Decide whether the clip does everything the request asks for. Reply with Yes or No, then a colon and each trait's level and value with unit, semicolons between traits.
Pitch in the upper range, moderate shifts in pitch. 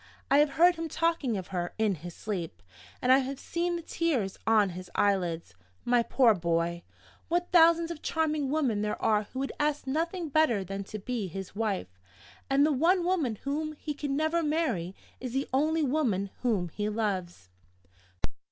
No: very high, 255 Hz; wide, 8.0 semitones